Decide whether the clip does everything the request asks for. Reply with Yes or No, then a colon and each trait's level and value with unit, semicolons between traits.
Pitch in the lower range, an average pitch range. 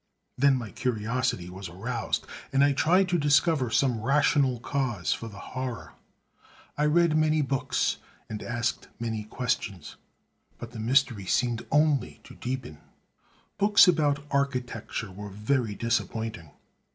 Yes: low, 125 Hz; average, 4.4 semitones